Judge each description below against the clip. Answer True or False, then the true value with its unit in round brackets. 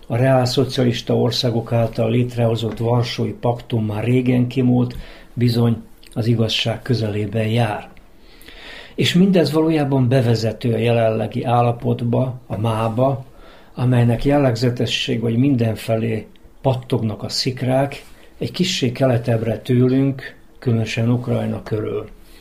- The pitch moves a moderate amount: False (2.2 semitones)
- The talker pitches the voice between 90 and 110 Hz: False (120 Hz)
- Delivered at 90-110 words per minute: True (105 wpm)